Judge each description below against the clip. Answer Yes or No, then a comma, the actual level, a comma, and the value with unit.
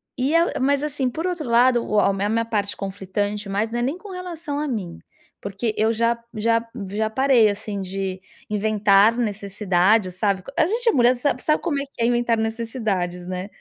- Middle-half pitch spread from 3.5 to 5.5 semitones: Yes, average, 4.6 semitones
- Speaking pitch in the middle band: No, high, 225 Hz